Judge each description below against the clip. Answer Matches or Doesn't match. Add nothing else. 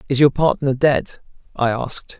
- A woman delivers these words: Doesn't match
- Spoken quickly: Doesn't match